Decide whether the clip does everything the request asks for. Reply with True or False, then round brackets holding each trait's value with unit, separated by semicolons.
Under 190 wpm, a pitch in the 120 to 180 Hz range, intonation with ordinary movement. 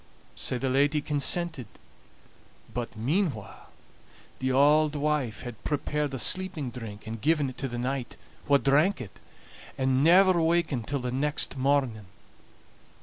True (135 wpm; 140 Hz; 3.3 semitones)